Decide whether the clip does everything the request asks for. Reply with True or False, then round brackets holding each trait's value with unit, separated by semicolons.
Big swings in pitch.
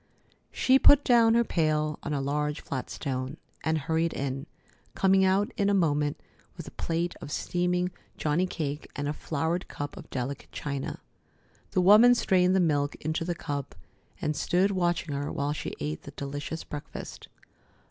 False (4.1 semitones)